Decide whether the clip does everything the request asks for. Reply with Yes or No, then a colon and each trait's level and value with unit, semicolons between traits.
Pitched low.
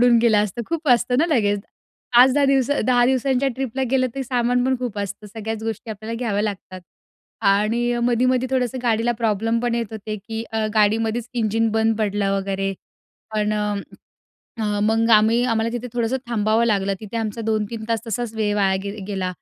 No: high, 225 Hz